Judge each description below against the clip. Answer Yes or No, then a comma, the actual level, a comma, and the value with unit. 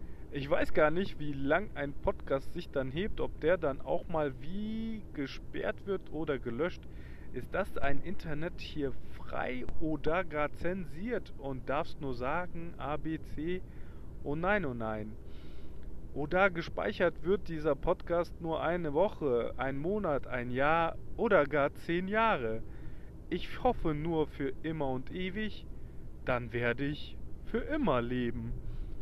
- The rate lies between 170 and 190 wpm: No, average, 145 wpm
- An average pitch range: No, wide, 6.0 semitones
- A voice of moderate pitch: Yes, medium, 150 Hz